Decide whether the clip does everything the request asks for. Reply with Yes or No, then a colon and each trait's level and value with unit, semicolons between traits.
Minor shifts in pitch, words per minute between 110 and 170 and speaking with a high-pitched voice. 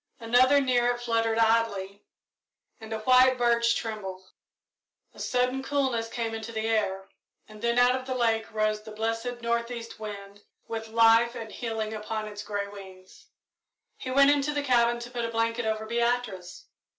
Yes: narrow, 2.0 semitones; average, 165 wpm; high, 230 Hz